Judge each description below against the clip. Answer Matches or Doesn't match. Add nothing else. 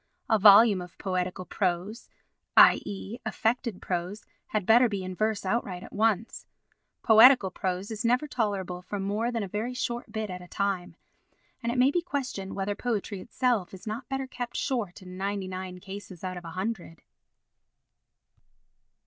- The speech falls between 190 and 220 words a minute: Doesn't match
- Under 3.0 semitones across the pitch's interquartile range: Doesn't match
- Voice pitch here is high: Matches